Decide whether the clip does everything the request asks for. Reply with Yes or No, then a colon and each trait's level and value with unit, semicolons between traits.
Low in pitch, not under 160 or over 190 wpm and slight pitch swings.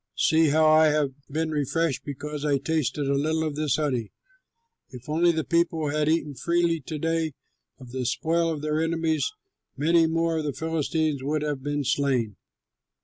No: medium, 155 Hz; average, 175 wpm; narrow, 2.2 semitones